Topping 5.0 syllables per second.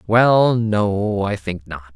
No: 2.9 syllables/s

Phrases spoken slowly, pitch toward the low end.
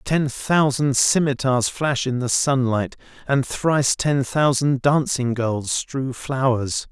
Yes: slow, 130 wpm; low, 130 Hz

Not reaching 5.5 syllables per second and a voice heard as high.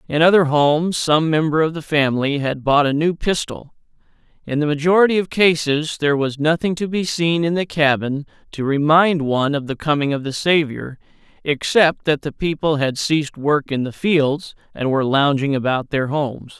No: 5.1 syllables/s; medium, 150 Hz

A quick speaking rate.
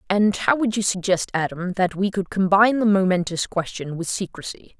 No: average, 190 wpm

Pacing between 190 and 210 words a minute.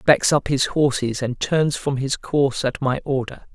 Yes: fast, 205 wpm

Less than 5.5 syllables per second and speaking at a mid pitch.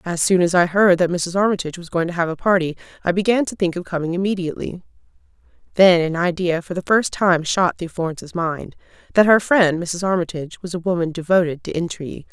No: 6.1 syllables/s; medium, 175 Hz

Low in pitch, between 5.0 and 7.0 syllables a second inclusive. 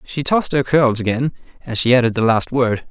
Yes: low, 125 Hz; 5.7 syllables/s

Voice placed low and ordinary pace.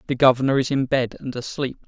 No: low, 130 Hz; fast, 225 wpm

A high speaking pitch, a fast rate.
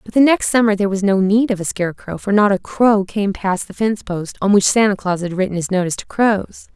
Yes: high, 200 Hz; fast, 265 wpm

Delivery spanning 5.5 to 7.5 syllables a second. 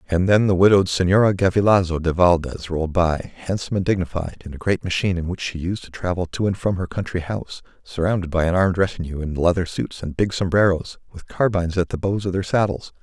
Yes: 6.2 syllables/s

